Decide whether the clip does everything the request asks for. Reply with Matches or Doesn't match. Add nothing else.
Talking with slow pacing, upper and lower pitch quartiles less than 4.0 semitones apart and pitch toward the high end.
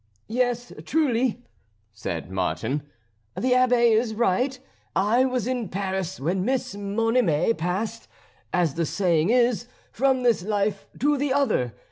Doesn't match